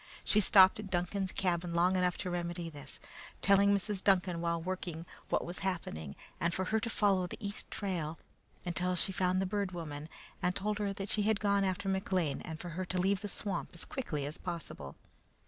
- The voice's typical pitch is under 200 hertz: Yes, medium, 185 Hz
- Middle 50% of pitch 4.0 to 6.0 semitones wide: No, narrow, 2.6 semitones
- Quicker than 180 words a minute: Yes, average, 200 wpm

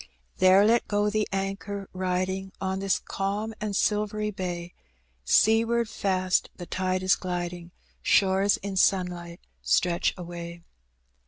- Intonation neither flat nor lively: No, narrow, 2.2 semitones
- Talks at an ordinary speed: No, slow, 120 wpm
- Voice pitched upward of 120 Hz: Yes, high, 190 Hz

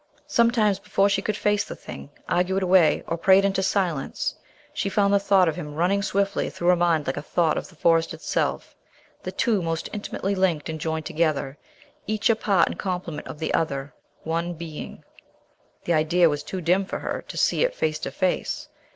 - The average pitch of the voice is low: No, medium, 180 Hz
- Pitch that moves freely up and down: No, average, 3.7 semitones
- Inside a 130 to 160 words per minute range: No, fast, 205 wpm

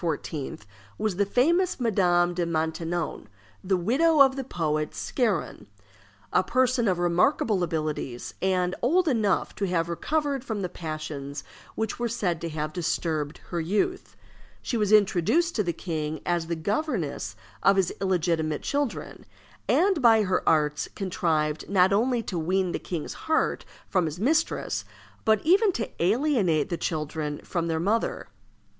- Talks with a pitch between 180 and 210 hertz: Yes, medium, 185 Hz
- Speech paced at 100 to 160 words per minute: Yes, average, 150 wpm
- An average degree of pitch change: No, wide, 6.2 semitones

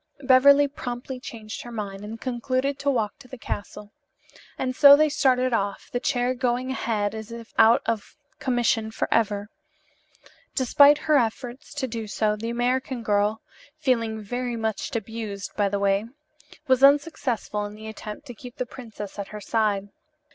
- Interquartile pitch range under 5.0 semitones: Yes, average, 3.4 semitones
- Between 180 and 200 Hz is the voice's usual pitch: No, high, 235 Hz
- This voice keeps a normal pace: Yes, average, 160 wpm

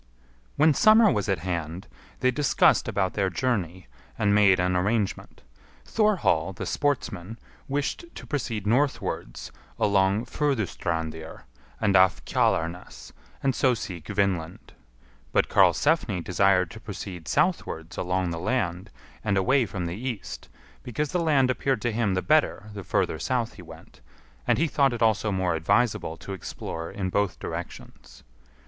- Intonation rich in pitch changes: Yes, wide, 6.0 semitones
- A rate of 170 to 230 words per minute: No, average, 145 wpm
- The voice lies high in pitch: No, low, 100 Hz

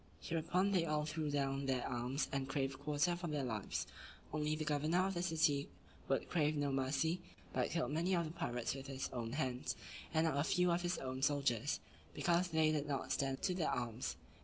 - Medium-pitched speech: Yes, medium, 150 Hz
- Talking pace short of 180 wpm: No, fast, 205 wpm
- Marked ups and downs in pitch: No, average, 3.6 semitones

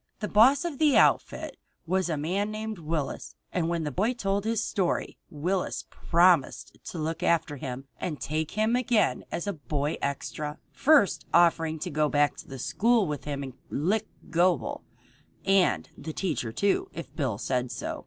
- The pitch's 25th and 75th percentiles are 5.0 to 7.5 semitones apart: Yes, wide, 5.5 semitones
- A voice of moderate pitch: Yes, medium, 170 Hz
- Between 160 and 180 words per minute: Yes, average, 175 wpm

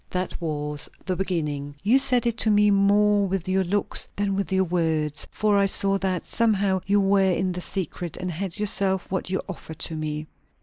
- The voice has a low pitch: No, high, 190 Hz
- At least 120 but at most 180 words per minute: No, average, 200 wpm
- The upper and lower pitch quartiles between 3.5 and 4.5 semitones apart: No, average, 2.8 semitones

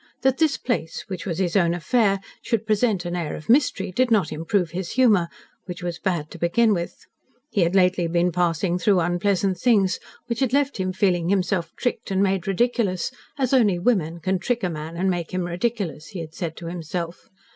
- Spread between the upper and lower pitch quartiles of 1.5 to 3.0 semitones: No, average, 3.8 semitones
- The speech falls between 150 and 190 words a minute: No, average, 200 wpm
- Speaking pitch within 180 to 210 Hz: Yes, medium, 185 Hz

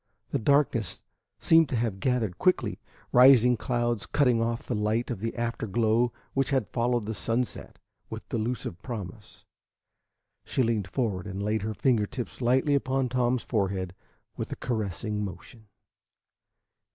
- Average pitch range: Yes, average, 3.0 semitones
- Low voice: Yes, low, 115 Hz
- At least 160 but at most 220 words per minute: No, average, 145 wpm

